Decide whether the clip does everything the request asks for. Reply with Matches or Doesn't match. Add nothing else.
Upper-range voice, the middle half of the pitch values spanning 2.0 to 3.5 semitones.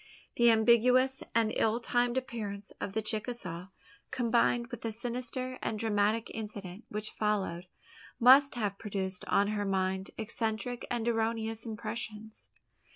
Matches